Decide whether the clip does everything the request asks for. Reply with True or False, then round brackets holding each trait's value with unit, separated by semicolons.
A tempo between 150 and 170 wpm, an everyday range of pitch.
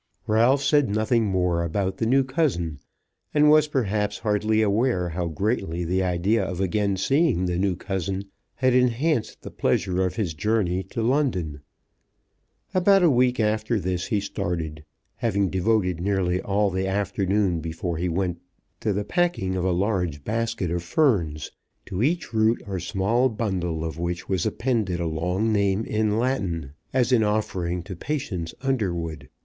True (160 wpm; 4.5 semitones)